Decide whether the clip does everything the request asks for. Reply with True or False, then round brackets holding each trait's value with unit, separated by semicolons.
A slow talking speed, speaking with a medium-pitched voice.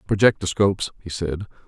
False (110 wpm; 95 Hz)